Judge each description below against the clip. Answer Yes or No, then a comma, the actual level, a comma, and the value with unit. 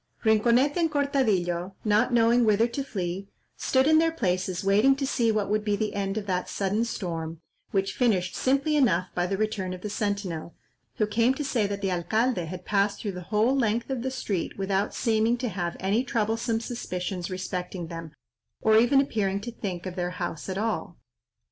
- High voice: Yes, high, 210 Hz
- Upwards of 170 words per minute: Yes, average, 190 wpm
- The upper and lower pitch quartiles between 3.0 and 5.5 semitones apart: Yes, average, 4.3 semitones